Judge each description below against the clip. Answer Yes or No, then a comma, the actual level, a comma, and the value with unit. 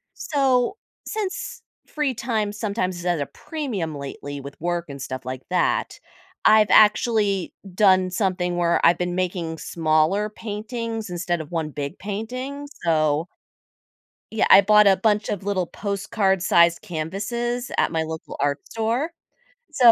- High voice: Yes, high, 195 Hz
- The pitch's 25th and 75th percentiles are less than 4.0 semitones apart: No, average, 4.9 semitones